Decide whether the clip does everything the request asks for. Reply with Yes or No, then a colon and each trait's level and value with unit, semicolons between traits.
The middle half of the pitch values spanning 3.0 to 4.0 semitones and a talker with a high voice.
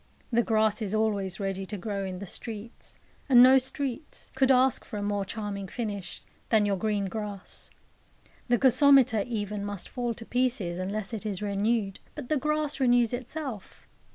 Yes: average, 3.7 semitones; high, 220 Hz